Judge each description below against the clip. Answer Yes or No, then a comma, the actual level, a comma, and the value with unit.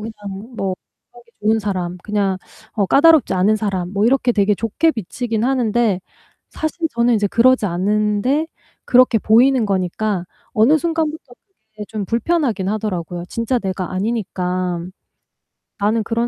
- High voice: Yes, high, 215 Hz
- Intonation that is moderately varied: Yes, average, 3.7 semitones